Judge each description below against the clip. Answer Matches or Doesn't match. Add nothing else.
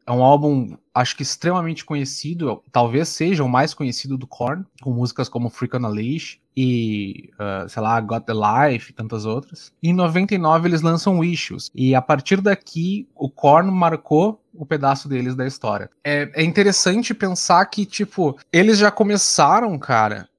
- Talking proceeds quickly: Doesn't match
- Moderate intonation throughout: Doesn't match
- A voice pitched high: Doesn't match